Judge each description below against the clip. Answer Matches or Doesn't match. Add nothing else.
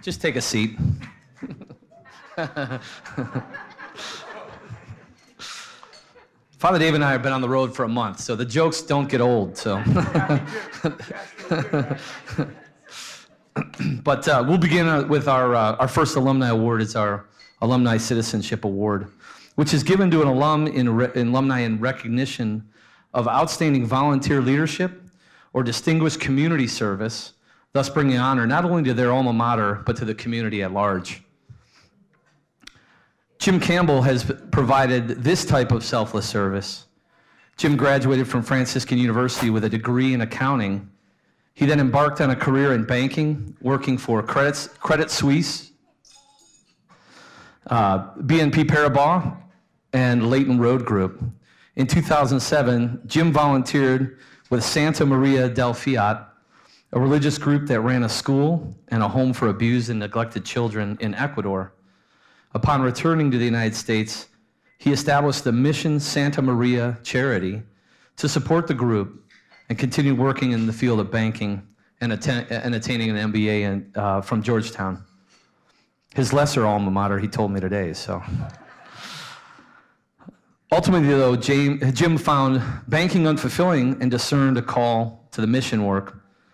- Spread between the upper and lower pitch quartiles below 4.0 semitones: Doesn't match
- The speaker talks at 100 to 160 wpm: Matches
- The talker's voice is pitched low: Matches